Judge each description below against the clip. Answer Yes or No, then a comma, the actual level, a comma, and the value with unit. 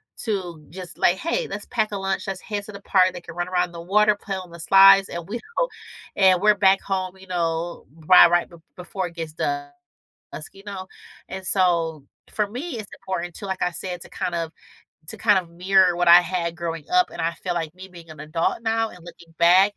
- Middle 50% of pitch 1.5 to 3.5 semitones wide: Yes, narrow, 2.4 semitones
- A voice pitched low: No, medium, 185 Hz